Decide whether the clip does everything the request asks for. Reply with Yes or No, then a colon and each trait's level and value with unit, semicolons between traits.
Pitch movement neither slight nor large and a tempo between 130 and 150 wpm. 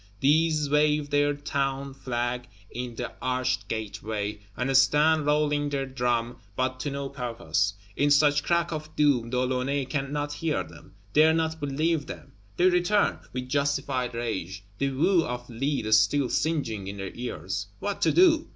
No: average, 3.4 semitones; average, 160 wpm